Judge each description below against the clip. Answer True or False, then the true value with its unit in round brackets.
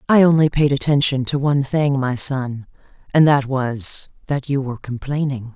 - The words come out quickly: False (175 wpm)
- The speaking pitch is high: False (135 Hz)